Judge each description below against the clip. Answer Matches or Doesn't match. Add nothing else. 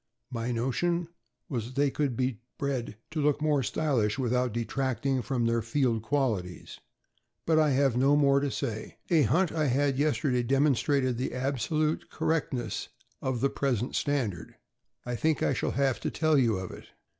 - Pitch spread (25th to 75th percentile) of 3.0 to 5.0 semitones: Matches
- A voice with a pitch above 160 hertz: Doesn't match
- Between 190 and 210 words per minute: Doesn't match